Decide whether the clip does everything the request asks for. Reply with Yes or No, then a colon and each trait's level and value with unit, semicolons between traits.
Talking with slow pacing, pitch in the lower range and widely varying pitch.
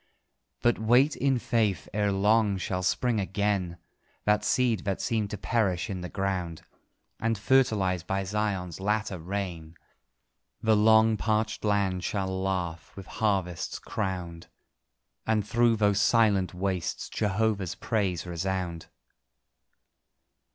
No: slow, 120 wpm; low, 100 Hz; average, 3.0 semitones